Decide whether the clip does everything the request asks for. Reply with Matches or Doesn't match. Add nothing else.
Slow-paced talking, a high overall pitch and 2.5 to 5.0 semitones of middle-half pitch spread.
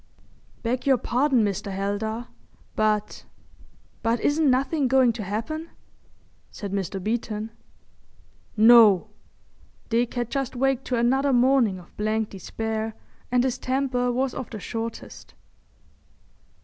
Matches